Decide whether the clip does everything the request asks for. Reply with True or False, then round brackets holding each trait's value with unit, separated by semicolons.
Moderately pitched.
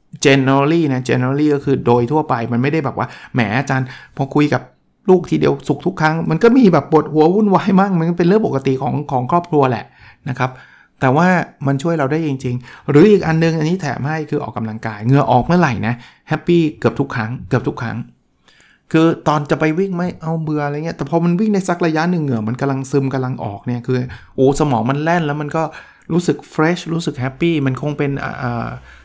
True (145 Hz)